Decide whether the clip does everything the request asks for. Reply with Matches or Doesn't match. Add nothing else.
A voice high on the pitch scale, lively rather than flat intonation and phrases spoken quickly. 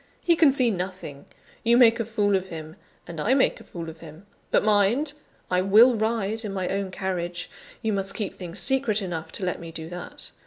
Doesn't match